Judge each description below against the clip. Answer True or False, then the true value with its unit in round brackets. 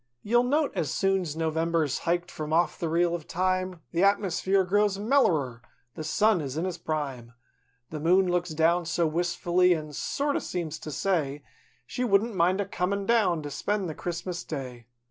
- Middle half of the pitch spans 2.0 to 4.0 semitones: True (3.6 semitones)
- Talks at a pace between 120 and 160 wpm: False (185 wpm)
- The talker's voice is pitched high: False (175 Hz)